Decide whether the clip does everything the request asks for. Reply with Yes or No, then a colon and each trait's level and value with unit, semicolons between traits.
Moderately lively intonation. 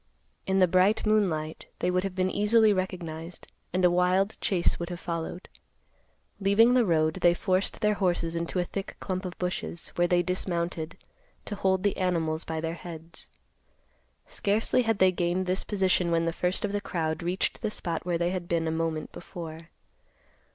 No: narrow, 2.3 semitones